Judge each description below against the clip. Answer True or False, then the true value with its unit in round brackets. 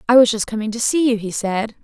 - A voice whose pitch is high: True (225 Hz)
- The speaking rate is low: False (295 wpm)